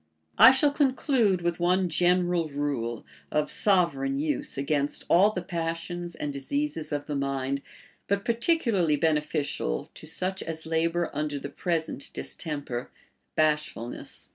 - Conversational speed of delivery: No, slow, 130 wpm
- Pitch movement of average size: Yes, average, 4.1 semitones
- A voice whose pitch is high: No, medium, 160 Hz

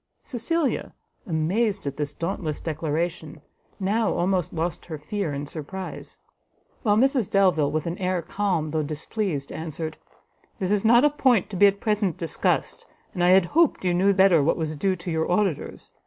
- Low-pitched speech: No, medium, 180 Hz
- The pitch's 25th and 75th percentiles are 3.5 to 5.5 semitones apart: Yes, average, 4.4 semitones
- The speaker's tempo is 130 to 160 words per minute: No, average, 175 wpm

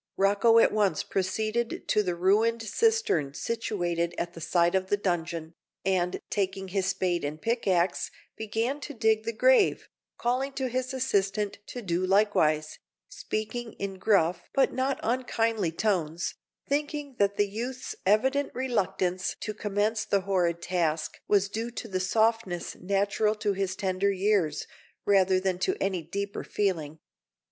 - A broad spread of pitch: No, average, 3.8 semitones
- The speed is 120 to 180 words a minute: Yes, average, 145 wpm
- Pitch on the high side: Yes, high, 200 Hz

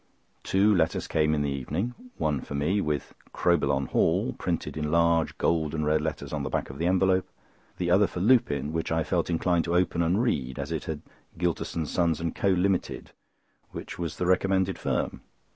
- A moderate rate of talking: Yes, average, 190 wpm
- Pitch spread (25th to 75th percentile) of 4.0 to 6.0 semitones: No, average, 3.2 semitones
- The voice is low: Yes, very low, 85 Hz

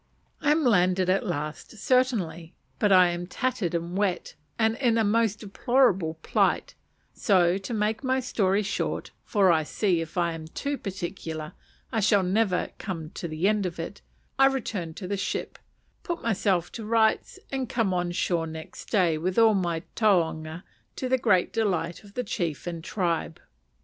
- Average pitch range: Yes, average, 4.5 semitones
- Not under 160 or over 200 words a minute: Yes, average, 175 wpm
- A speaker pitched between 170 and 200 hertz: Yes, high, 190 Hz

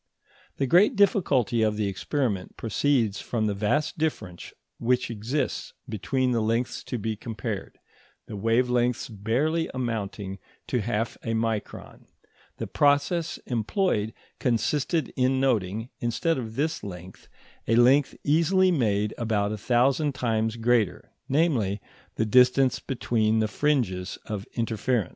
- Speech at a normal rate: No, slow, 130 wpm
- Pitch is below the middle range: Yes, low, 120 Hz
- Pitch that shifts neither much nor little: Yes, average, 4.1 semitones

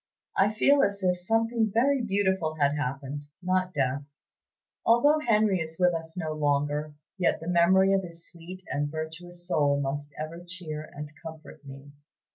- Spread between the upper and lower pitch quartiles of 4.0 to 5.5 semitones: Yes, average, 4.3 semitones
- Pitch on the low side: No, medium, 170 Hz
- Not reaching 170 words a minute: Yes, average, 160 wpm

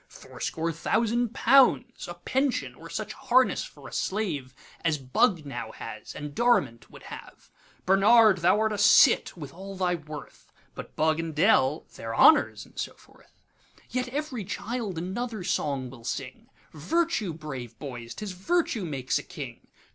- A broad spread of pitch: Yes, wide, 7.7 semitones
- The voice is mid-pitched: Yes, medium, 175 Hz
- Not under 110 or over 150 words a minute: Yes, average, 140 wpm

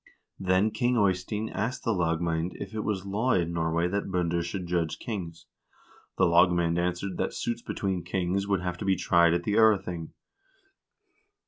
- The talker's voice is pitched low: Yes, very low, 90 Hz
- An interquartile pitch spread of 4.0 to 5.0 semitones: No, average, 2.9 semitones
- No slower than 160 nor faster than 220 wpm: Yes, average, 170 wpm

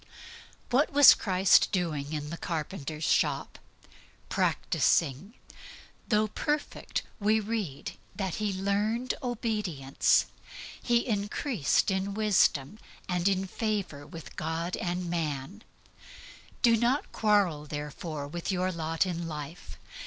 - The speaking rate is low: Yes, slow, 105 wpm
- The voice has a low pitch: No, high, 190 Hz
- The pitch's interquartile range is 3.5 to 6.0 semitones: Yes, average, 5.3 semitones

